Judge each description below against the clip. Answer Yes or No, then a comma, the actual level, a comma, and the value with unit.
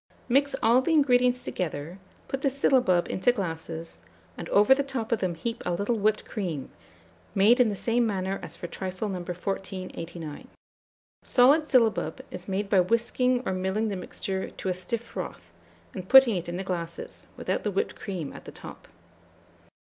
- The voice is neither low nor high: No, high, 200 Hz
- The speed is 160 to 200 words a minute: Yes, average, 175 wpm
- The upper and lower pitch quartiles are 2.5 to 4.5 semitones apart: No, average, 5.1 semitones